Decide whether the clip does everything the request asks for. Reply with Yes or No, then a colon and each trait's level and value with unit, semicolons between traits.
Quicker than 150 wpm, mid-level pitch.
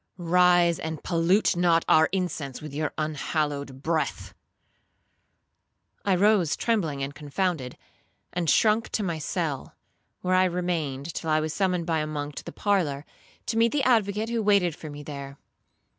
Yes: average, 160 wpm; medium, 165 Hz